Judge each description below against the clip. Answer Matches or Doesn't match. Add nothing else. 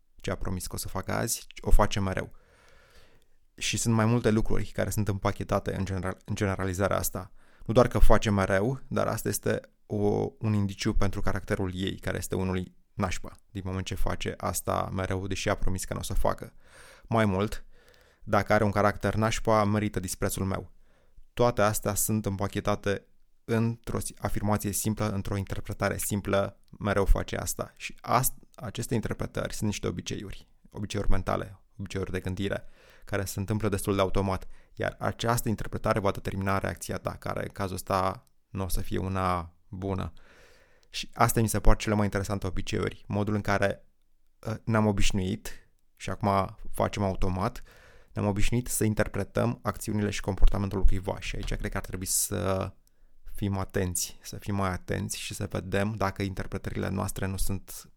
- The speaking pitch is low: Matches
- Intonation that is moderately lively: Doesn't match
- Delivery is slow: Doesn't match